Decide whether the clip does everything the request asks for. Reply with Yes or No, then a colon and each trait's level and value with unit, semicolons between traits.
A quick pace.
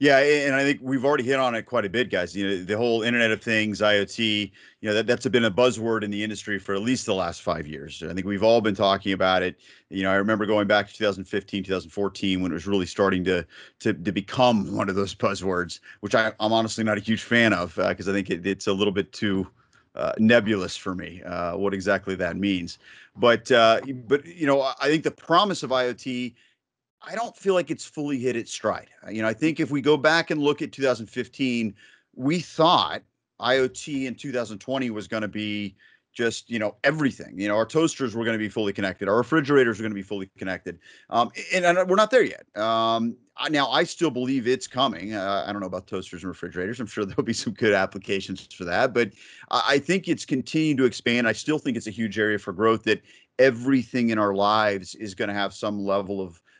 Yes: fast, 235 wpm